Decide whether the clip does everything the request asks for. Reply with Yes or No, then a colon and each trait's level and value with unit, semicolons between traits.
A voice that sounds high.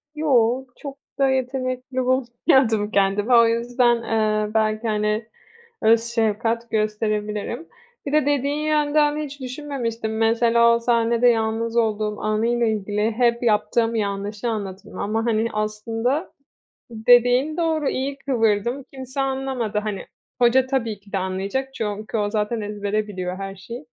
Yes: high, 230 Hz